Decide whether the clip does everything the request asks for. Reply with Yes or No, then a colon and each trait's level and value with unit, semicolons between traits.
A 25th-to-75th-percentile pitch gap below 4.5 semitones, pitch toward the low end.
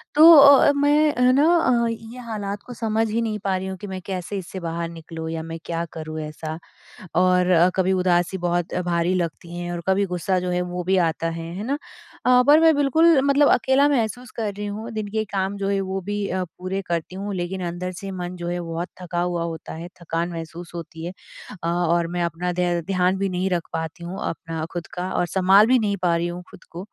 No: average, 3.4 semitones; medium, 185 Hz